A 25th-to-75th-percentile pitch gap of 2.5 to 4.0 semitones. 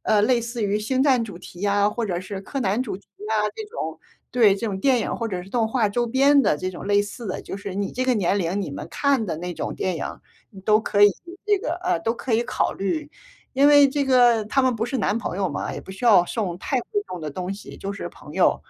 No: average, 4.6 semitones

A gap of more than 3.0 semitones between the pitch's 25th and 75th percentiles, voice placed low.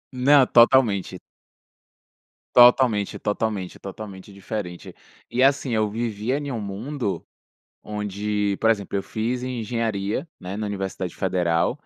Yes: average, 3.5 semitones; low, 105 Hz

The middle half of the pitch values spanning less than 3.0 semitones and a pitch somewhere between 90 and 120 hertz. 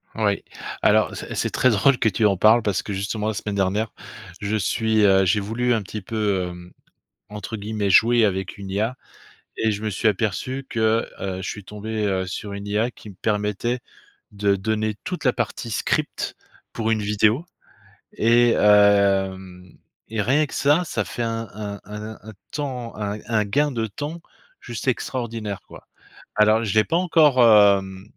Yes: narrow, 2.4 semitones; low, 105 Hz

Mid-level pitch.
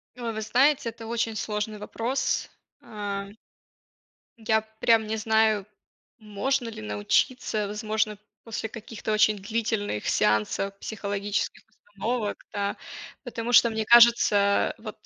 No: high, 220 Hz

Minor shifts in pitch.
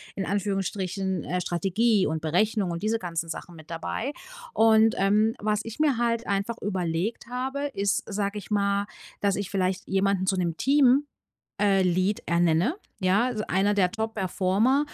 No: average, 3.2 semitones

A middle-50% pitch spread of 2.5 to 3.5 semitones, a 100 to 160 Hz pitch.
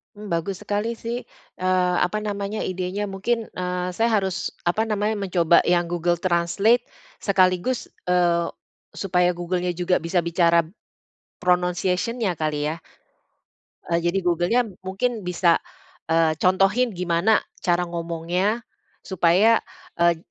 No: average, 2.8 semitones; medium, 180 Hz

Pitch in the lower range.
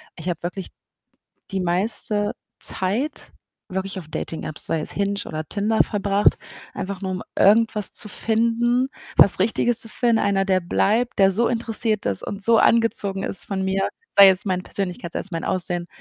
No: high, 200 Hz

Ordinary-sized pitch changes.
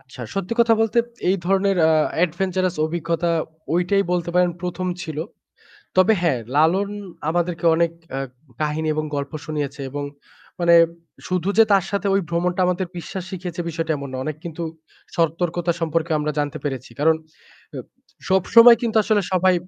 Yes: average, 3.0 semitones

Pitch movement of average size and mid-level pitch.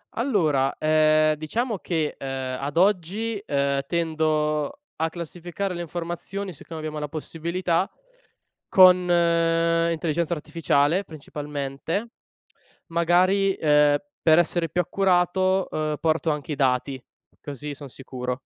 Yes: average, 3.1 semitones; medium, 165 Hz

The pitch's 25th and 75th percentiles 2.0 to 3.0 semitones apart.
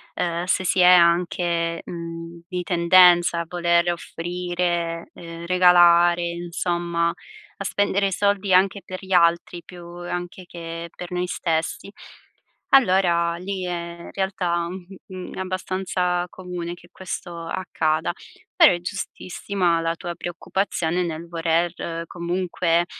No: narrow, 1.2 semitones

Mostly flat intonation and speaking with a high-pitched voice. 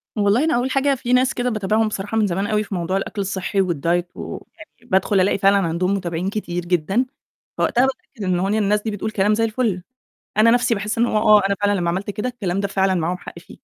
No: average, 3.0 semitones; high, 205 Hz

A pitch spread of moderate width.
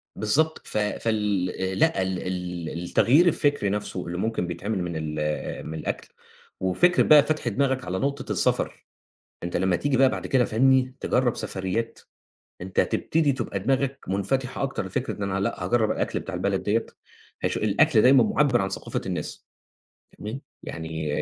No: wide, 6.2 semitones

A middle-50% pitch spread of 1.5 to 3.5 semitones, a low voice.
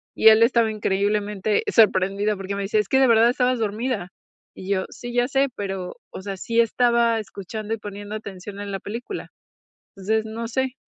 No: average, 2.8 semitones; high, 215 Hz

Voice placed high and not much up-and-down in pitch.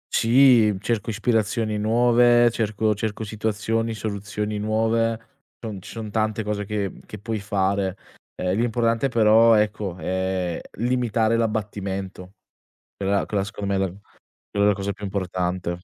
No: low, 105 Hz; narrow, 2.3 semitones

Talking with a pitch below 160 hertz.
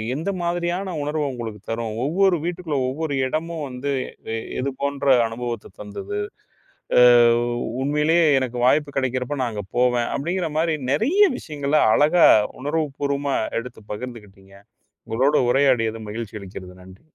Yes: medium, 140 Hz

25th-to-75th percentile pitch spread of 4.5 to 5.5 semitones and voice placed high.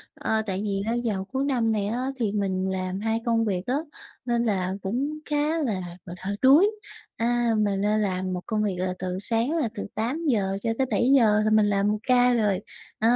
No: average, 3.7 semitones; high, 215 Hz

